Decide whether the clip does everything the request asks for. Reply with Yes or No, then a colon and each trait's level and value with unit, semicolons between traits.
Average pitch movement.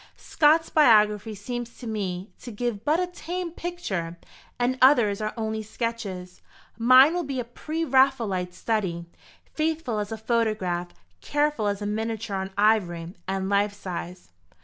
Yes: average, 4.7 semitones